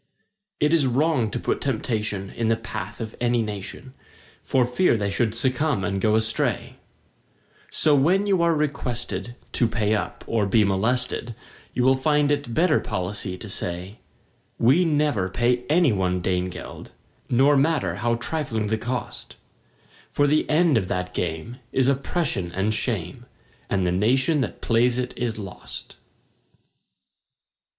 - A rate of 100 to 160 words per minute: Yes, average, 150 wpm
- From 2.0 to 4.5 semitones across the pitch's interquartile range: No, average, 5.1 semitones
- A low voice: Yes, low, 120 Hz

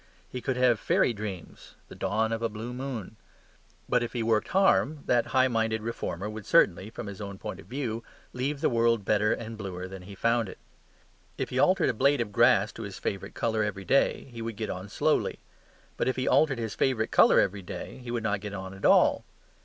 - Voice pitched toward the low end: Yes, low, 110 Hz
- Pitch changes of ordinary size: Yes, average, 3.4 semitones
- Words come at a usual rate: No, fast, 220 wpm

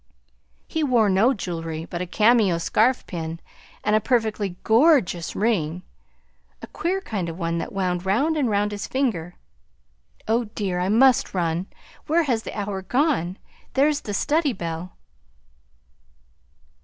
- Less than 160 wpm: Yes, average, 145 wpm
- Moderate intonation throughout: No, wide, 5.7 semitones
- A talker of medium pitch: No, high, 205 Hz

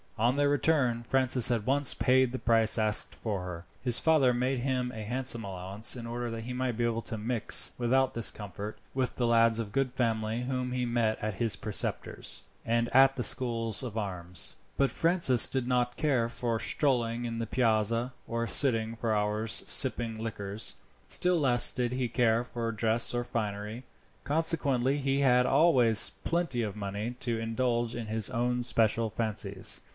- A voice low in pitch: Yes, low, 120 Hz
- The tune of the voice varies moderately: No, narrow, 2.3 semitones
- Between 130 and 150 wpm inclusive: No, average, 175 wpm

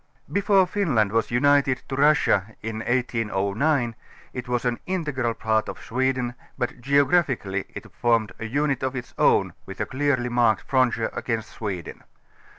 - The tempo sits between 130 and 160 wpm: Yes, average, 150 wpm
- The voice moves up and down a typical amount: Yes, average, 3.8 semitones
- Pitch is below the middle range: Yes, low, 125 Hz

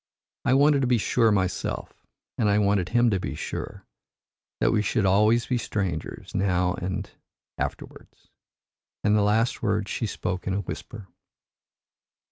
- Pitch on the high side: No, low, 105 Hz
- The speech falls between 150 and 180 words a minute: Yes, average, 155 wpm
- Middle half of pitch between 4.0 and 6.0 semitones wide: No, average, 3.2 semitones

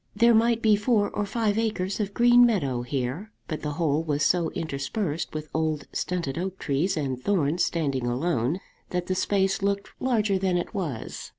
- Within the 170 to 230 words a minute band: Yes, average, 180 wpm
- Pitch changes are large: Yes, wide, 5.7 semitones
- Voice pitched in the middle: Yes, medium, 180 Hz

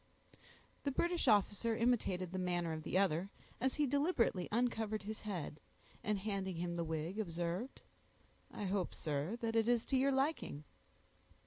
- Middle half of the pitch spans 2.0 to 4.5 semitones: No, average, 5.3 semitones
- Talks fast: No, average, 150 wpm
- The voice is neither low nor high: No, high, 205 Hz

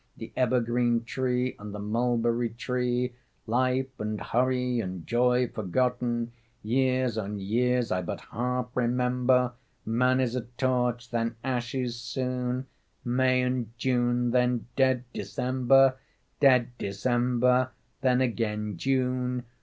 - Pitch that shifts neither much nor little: No, narrow, 1.3 semitones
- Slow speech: Yes, slow, 115 wpm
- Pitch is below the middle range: Yes, low, 125 Hz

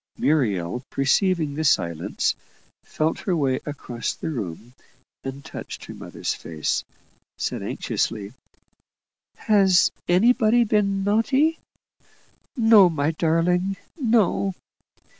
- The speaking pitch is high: No, medium, 165 Hz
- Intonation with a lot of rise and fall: Yes, wide, 7.6 semitones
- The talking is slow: Yes, slow, 100 wpm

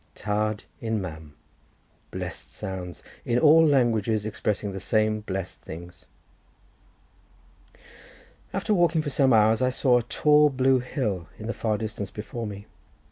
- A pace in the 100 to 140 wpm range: Yes, slow, 135 wpm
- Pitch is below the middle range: Yes, low, 110 Hz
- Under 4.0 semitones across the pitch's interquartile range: No, average, 4.3 semitones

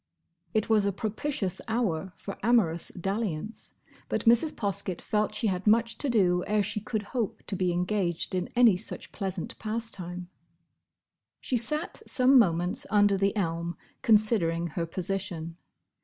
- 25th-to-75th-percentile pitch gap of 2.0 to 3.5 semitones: No, average, 3.9 semitones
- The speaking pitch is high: Yes, high, 200 Hz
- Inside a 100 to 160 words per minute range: Yes, average, 145 wpm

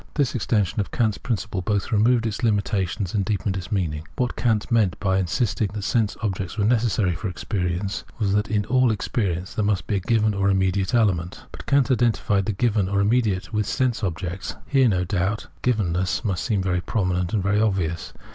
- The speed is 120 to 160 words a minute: No, average, 190 wpm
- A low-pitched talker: Yes, low, 100 Hz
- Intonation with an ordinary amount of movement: Yes, average, 3.0 semitones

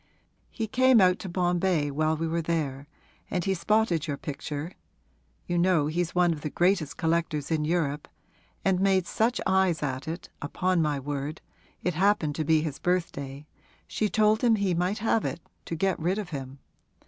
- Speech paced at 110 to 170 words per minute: No, average, 185 wpm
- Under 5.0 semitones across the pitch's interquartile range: Yes, average, 3.9 semitones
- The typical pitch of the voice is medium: Yes, medium, 170 Hz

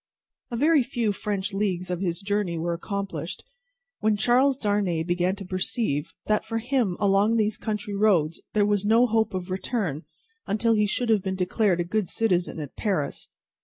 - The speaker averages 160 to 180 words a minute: Yes, average, 175 wpm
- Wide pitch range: No, average, 3.3 semitones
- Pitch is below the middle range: No, high, 205 Hz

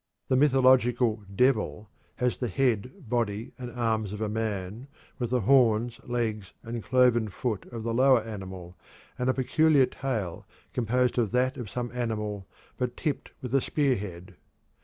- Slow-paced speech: No, average, 155 wpm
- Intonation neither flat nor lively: Yes, average, 3.0 semitones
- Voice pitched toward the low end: Yes, low, 120 Hz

